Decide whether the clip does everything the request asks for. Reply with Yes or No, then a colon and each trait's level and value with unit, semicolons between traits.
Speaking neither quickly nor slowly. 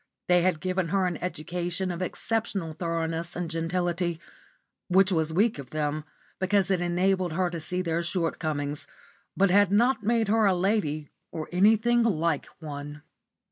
Yes: average, 155 wpm